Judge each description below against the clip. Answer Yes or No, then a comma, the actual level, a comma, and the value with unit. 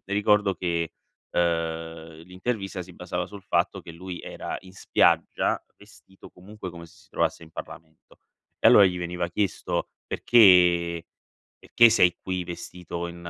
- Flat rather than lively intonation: Yes, narrow, 2.0 semitones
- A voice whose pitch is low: Yes, very low, 90 Hz